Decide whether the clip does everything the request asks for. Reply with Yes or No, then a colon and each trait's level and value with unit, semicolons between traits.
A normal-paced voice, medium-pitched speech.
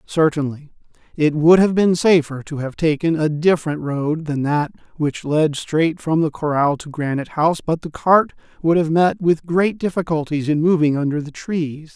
Yes: average, 185 wpm; medium, 155 Hz